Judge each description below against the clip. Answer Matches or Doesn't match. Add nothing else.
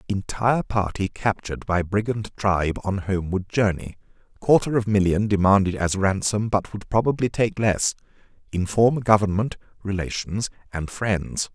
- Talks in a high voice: Doesn't match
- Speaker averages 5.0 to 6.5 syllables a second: Doesn't match